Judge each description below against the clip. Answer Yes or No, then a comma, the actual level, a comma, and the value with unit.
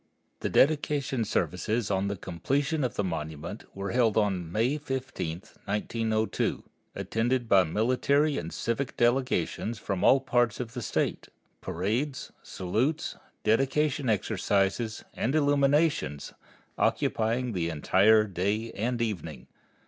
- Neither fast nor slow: No, slow, 120 wpm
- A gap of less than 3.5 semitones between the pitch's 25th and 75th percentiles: No, average, 5.3 semitones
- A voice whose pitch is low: Yes, low, 110 Hz